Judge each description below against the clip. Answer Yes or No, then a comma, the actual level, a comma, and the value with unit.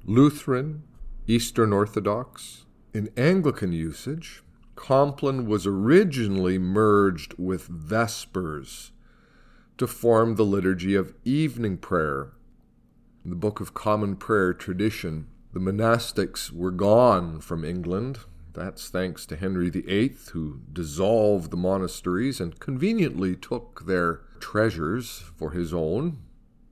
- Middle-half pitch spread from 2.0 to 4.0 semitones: No, average, 4.5 semitones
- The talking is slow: Yes, slow, 110 wpm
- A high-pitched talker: No, low, 100 Hz